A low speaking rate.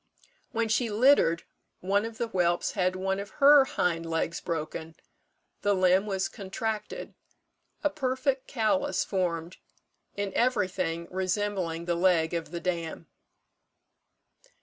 Yes: slow, 125 wpm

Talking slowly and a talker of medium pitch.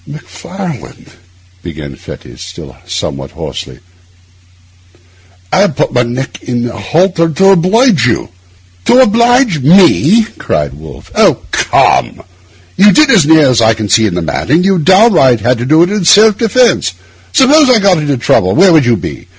No: average, 160 wpm; medium, 160 Hz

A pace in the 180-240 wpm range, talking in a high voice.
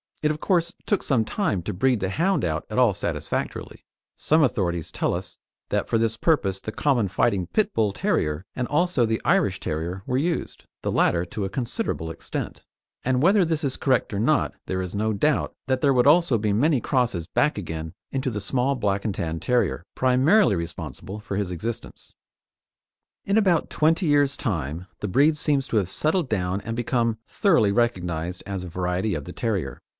No: average, 190 wpm; low, 115 Hz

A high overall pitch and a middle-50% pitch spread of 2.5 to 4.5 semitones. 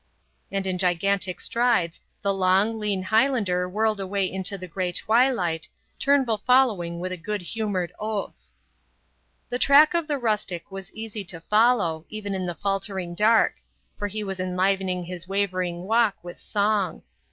Yes: high, 195 Hz; average, 3.1 semitones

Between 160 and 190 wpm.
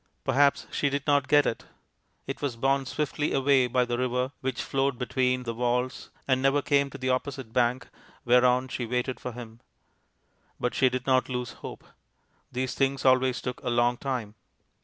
Yes: average, 180 wpm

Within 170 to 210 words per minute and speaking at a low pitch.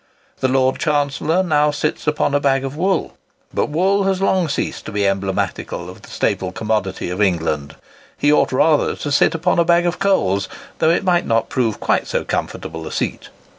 No: average, 195 wpm; medium, 145 Hz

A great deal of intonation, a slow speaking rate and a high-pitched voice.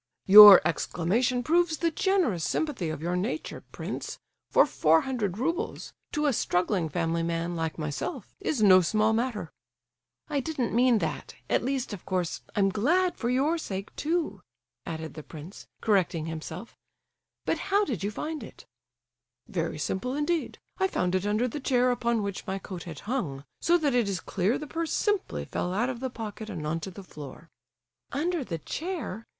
No: wide, 7.9 semitones; average, 170 wpm; high, 215 Hz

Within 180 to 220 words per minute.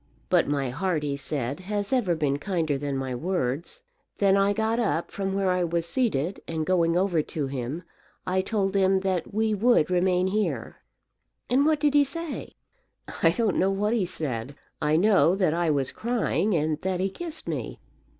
Yes: average, 185 wpm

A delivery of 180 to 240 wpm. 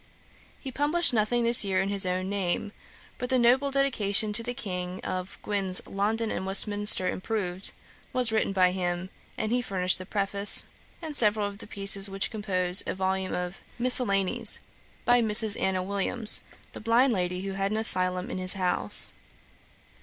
No: average, 170 wpm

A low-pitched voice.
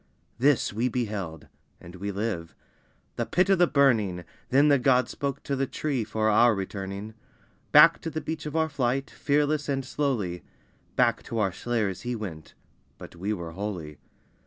Yes: low, 120 Hz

